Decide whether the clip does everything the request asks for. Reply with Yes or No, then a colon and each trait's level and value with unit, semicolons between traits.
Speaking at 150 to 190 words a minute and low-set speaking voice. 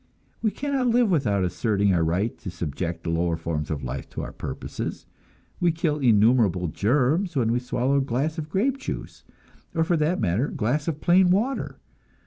Yes: average, 185 wpm; low, 125 Hz